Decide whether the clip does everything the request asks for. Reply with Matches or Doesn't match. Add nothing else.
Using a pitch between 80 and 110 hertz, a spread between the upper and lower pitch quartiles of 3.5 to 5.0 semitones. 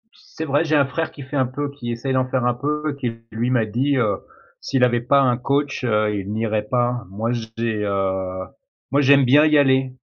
Doesn't match